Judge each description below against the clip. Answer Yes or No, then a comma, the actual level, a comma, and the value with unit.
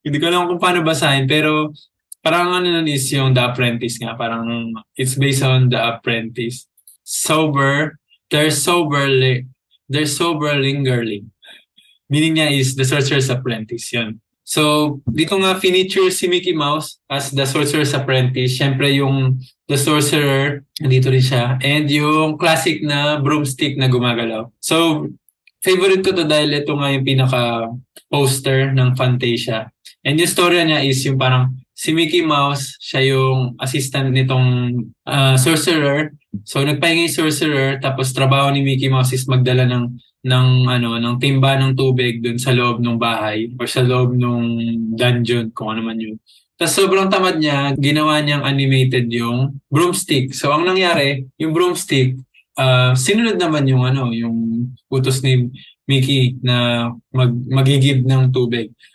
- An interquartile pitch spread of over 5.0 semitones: No, average, 3.2 semitones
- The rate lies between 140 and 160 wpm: Yes, average, 150 wpm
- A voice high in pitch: No, low, 135 Hz